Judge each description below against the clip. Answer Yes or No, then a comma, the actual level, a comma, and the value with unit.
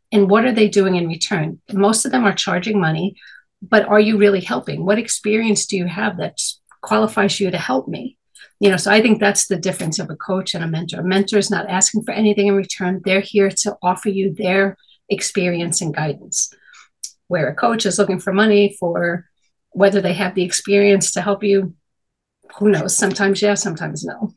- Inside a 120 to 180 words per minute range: No, fast, 205 wpm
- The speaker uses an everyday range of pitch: No, narrow, 1.9 semitones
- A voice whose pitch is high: Yes, high, 195 Hz